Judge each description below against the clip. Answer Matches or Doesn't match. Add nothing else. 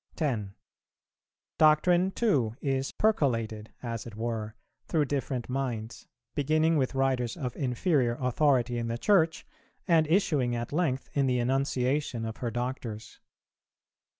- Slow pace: Matches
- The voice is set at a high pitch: Doesn't match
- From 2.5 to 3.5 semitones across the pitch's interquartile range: Doesn't match